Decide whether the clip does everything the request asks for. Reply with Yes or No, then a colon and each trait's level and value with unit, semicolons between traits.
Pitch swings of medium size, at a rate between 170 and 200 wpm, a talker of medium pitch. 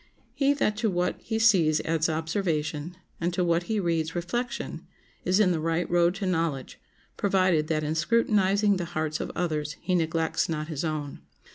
Yes: average, 3.5 semitones; average, 175 wpm; medium, 170 Hz